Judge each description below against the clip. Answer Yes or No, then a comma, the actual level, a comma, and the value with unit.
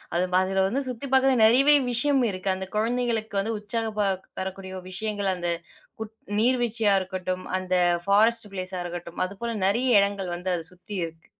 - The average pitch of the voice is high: Yes, high, 205 Hz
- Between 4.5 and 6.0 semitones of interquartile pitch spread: No, average, 3.8 semitones